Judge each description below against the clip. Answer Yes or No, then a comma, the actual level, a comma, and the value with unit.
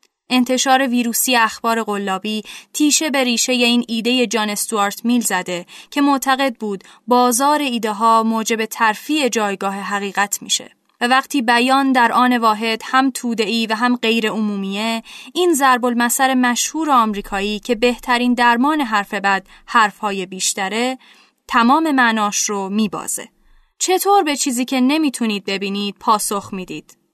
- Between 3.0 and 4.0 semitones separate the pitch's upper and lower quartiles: Yes, average, 3.7 semitones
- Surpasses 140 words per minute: No, average, 135 wpm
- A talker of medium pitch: No, high, 235 Hz